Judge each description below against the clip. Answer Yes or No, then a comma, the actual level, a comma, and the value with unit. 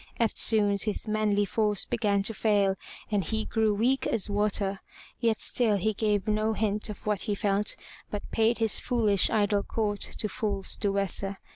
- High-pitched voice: Yes, high, 210 Hz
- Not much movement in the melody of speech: Yes, narrow, 1.5 semitones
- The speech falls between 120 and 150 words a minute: No, average, 165 wpm